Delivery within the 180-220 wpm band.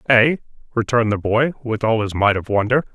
Yes: fast, 205 wpm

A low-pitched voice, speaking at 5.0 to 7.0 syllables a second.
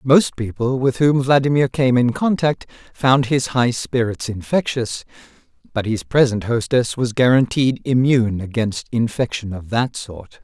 No: low, 120 Hz; 4.5 syllables/s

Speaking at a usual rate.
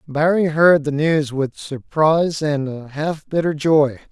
Yes: average, 160 wpm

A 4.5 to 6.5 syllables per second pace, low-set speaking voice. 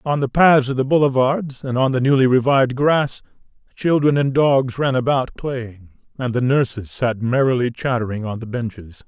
Yes: 5.0 syllables/s; low, 130 Hz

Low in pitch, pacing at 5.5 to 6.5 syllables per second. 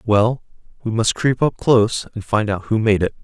No: low, 110 Hz; 5.0 syllables/s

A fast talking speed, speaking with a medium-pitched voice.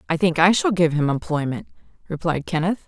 No: average, 190 wpm; medium, 170 Hz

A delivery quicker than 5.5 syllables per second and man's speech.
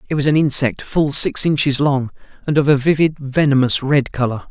No: 5.3 syllables/s; male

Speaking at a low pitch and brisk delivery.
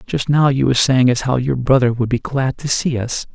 Yes: low, 130 Hz; fast, 270 wpm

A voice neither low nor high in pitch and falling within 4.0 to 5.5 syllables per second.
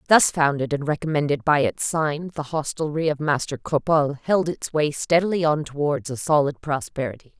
Yes: medium, 150 Hz; 5.2 syllables/s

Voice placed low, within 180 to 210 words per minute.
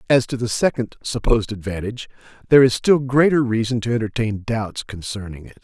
No: low, 115 Hz; average, 170 wpm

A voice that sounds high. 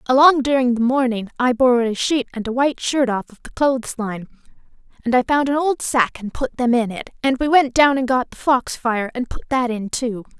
Yes: very high, 250 Hz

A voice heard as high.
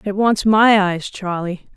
Yes: high, 200 Hz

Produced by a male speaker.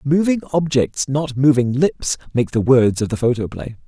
Yes: male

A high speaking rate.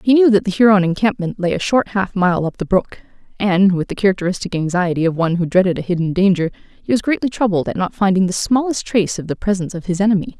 Yes: fast, 240 wpm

